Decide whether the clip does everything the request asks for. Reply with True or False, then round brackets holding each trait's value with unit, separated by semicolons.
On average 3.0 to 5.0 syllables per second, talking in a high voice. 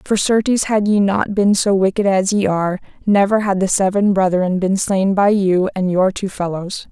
True (4.8 syllables/s; 195 Hz)